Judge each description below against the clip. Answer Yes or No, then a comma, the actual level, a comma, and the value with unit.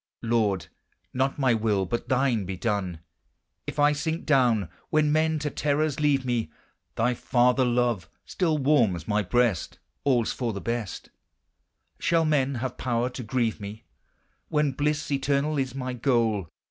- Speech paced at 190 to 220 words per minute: No, average, 150 wpm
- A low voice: Yes, low, 125 Hz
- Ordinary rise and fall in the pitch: Yes, average, 4.3 semitones